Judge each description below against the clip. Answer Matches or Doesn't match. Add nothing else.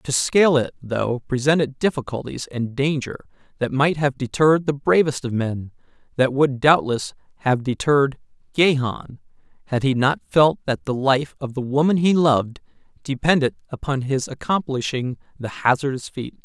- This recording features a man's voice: Matches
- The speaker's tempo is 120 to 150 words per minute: Matches